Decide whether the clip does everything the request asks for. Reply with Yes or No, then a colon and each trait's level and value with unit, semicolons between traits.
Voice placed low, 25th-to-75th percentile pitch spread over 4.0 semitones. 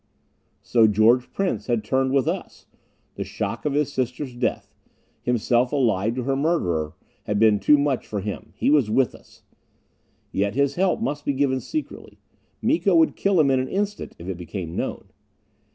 Yes: low, 130 Hz; average, 5.1 semitones